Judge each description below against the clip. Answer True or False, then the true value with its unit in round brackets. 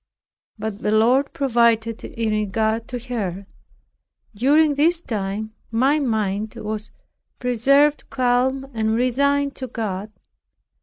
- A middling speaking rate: False (110 wpm)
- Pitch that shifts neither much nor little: True (3.6 semitones)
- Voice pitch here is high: True (230 Hz)